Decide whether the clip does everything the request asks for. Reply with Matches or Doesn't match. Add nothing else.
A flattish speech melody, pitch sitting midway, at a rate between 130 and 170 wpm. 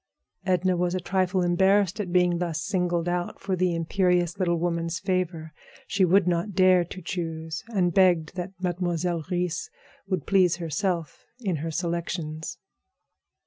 Matches